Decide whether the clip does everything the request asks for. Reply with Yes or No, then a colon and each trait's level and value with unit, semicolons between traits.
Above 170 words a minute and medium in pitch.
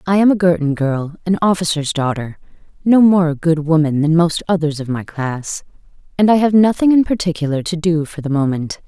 Yes: fast, 205 wpm; medium, 165 Hz